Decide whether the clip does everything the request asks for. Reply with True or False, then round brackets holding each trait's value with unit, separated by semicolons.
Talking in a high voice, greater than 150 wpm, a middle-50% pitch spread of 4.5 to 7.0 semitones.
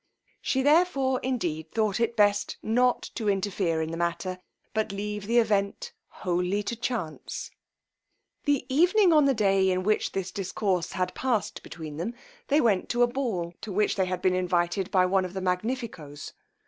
True (200 Hz; 175 wpm; 4.8 semitones)